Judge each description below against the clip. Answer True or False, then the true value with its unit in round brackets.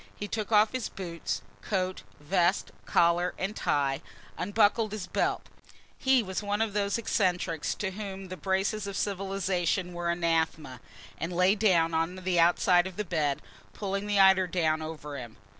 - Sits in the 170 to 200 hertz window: True (185 Hz)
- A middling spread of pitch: True (3.1 semitones)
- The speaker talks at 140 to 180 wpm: True (160 wpm)